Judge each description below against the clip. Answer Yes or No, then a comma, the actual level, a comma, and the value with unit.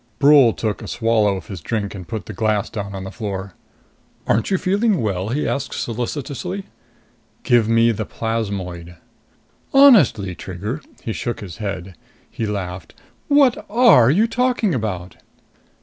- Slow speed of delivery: No, average, 150 wpm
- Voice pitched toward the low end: Yes, low, 110 Hz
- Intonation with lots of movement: Yes, wide, 6.6 semitones